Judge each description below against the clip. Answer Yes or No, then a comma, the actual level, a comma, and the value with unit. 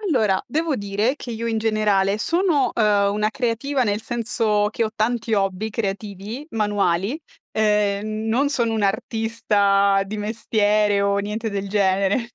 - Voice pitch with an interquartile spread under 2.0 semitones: No, narrow, 2.4 semitones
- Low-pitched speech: No, high, 215 Hz